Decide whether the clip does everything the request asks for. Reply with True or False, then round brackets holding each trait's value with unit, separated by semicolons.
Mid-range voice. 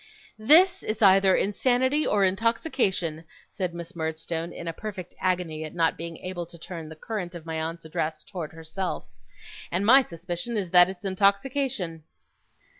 True (180 Hz)